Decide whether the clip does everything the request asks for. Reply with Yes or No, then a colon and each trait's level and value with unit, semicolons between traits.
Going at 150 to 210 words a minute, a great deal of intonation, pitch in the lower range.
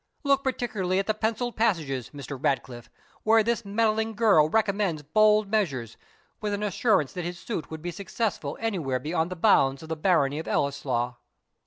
No: average, 170 wpm; wide, 7.0 semitones; medium, 185 Hz